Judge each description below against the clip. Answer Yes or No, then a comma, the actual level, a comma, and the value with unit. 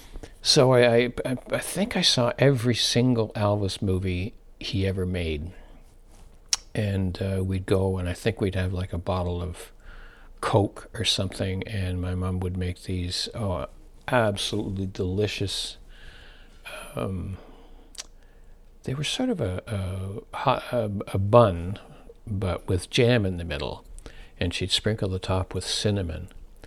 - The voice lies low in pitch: Yes, very low, 95 Hz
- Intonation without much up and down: No, average, 3.0 semitones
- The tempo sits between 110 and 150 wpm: Yes, average, 140 wpm